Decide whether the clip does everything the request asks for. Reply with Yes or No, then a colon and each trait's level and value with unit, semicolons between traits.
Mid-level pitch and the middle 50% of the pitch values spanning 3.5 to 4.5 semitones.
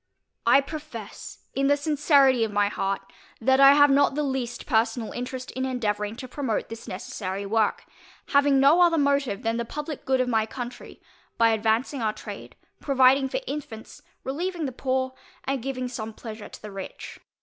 No: very high, 255 Hz; average, 3.9 semitones